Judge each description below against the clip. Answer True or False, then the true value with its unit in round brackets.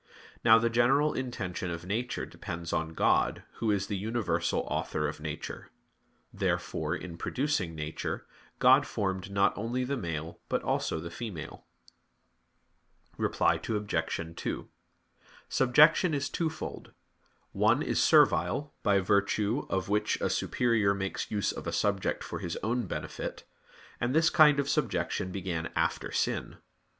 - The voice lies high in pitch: False (100 Hz)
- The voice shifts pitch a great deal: True (5.8 semitones)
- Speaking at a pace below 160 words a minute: True (140 wpm)